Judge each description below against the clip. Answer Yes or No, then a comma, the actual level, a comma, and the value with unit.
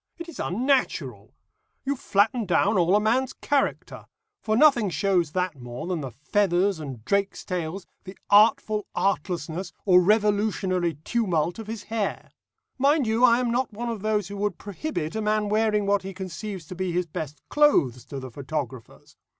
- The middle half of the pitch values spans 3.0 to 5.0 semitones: Yes, average, 4.2 semitones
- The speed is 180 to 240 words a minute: No, average, 170 wpm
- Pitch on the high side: Yes, high, 200 Hz